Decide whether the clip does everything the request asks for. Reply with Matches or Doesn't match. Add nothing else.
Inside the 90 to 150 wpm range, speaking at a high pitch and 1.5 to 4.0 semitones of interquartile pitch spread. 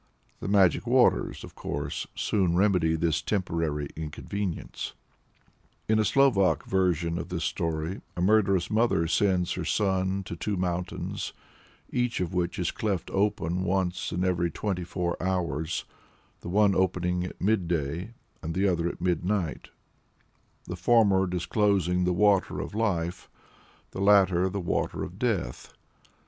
Doesn't match